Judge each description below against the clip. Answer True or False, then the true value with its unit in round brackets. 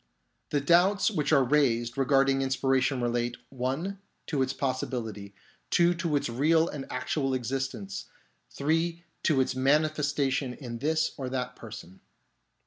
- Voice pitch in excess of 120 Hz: True (135 Hz)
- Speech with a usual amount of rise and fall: True (3.4 semitones)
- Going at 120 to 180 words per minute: True (135 wpm)